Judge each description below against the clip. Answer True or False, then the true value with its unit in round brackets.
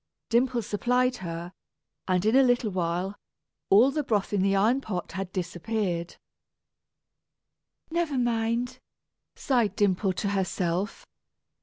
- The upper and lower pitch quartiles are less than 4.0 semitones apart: False (4.8 semitones)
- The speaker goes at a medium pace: False (120 wpm)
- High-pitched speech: True (205 Hz)